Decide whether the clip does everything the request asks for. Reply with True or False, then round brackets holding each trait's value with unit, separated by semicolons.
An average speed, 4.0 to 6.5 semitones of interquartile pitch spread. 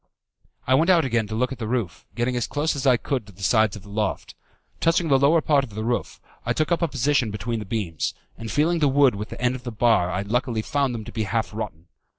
False (265 wpm; 4.4 semitones)